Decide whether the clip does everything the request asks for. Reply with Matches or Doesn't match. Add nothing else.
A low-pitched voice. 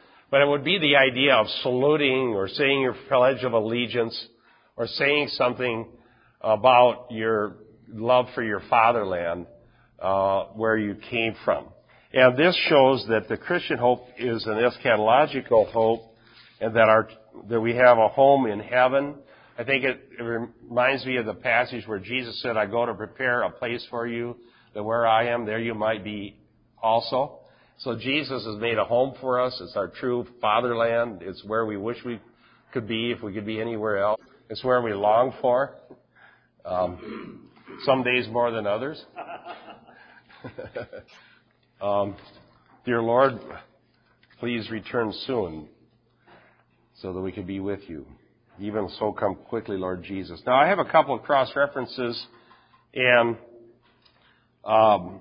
Matches